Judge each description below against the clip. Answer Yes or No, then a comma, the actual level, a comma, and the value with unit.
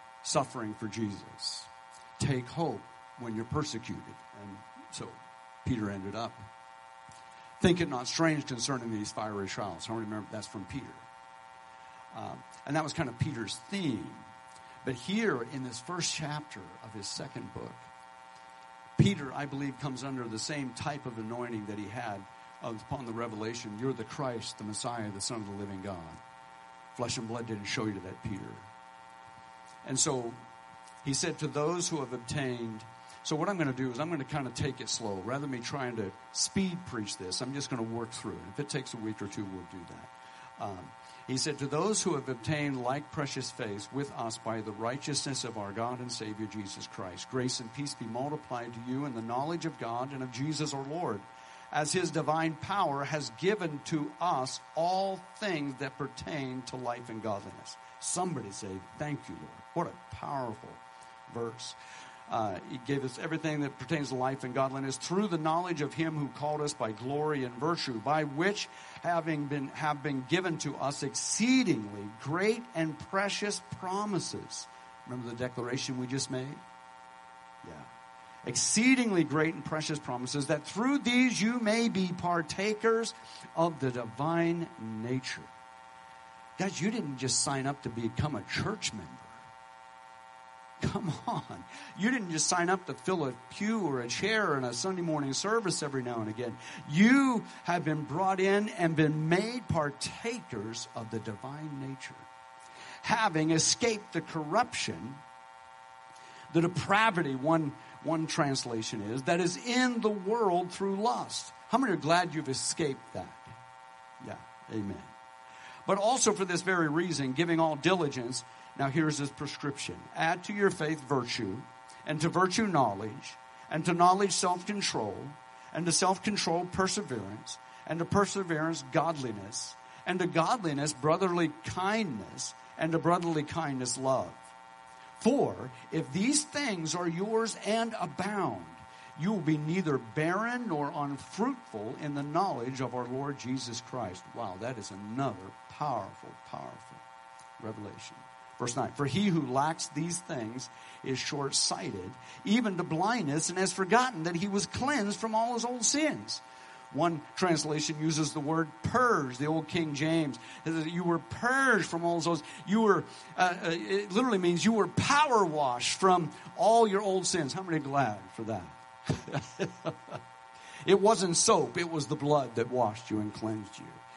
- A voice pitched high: No, low, 135 Hz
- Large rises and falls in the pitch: Yes, wide, 8.5 semitones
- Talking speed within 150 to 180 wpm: Yes, average, 165 wpm